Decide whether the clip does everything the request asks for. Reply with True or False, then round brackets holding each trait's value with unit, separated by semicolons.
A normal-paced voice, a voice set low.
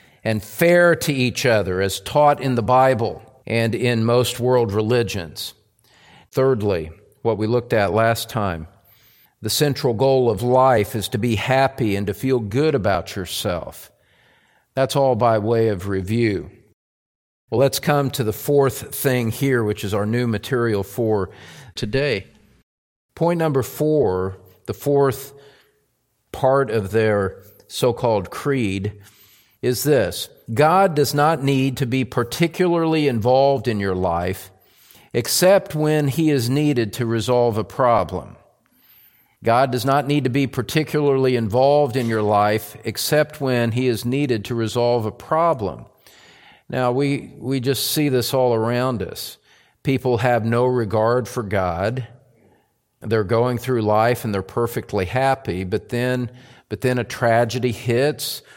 True (145 wpm; 120 Hz)